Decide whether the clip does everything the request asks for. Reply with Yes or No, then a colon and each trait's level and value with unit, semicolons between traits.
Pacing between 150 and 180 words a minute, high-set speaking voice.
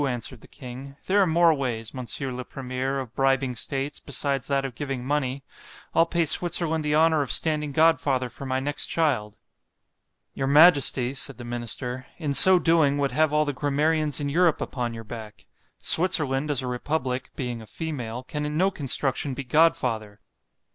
No: average, 165 wpm; medium, 140 Hz